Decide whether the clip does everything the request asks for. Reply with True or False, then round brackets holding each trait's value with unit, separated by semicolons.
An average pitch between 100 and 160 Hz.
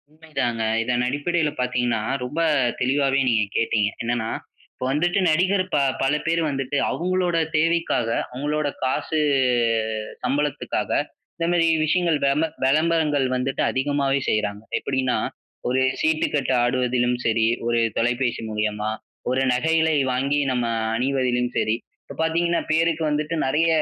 True (135 Hz)